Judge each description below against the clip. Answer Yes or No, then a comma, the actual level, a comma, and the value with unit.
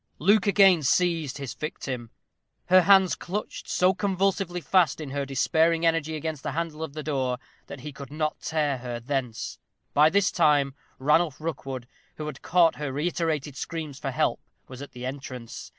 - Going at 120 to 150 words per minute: No, average, 170 wpm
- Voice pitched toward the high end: No, medium, 150 Hz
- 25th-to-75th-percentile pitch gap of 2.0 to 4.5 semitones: Yes, average, 3.7 semitones